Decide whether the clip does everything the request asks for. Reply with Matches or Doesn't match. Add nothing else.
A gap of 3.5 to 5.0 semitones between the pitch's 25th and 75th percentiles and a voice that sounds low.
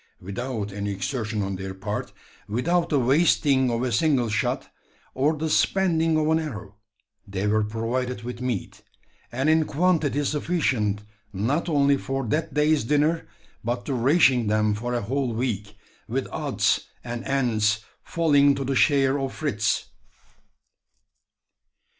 Doesn't match